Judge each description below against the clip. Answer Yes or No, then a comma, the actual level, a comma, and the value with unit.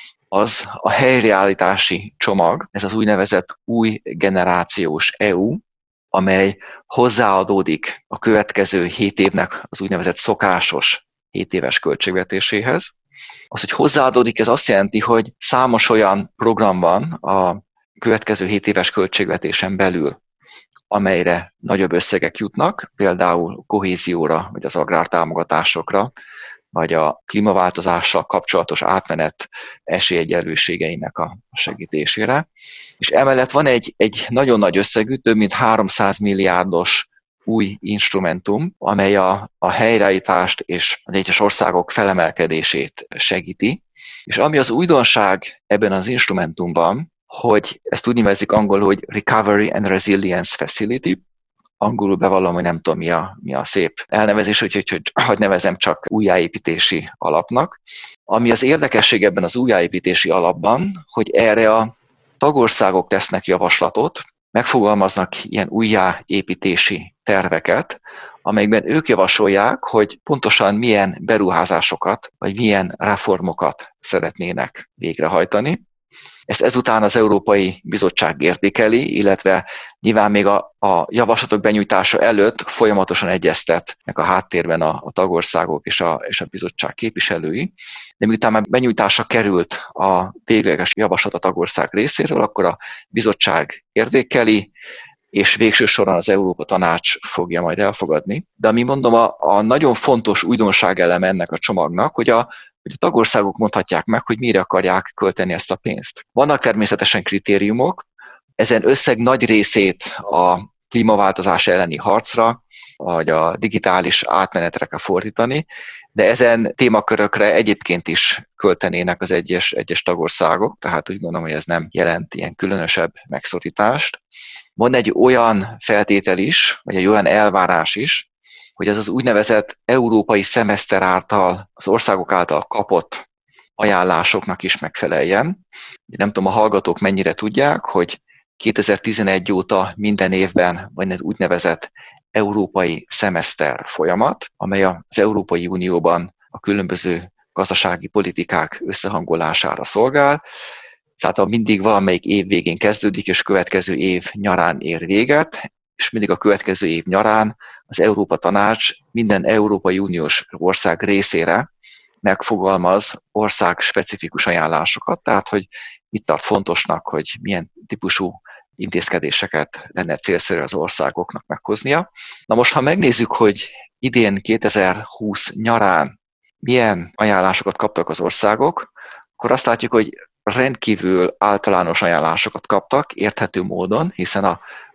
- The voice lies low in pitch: Yes, low, 100 Hz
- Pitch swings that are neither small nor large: Yes, average, 3.0 semitones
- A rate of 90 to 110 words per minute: No, average, 125 wpm